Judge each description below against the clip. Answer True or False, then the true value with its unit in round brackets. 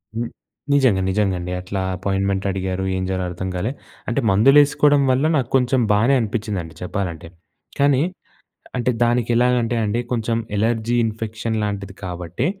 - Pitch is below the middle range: True (110 Hz)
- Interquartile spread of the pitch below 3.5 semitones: False (4.2 semitones)